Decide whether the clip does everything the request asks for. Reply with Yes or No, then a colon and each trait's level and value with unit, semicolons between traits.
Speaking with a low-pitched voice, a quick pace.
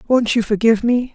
No: high, 230 Hz; fast, 210 wpm